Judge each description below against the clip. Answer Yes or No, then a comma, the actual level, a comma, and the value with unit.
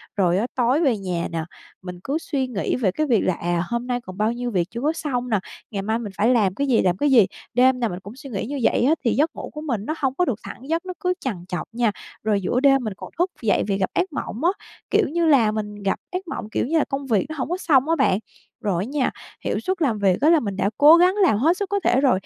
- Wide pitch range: Yes, wide, 6.6 semitones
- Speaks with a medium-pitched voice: No, high, 245 Hz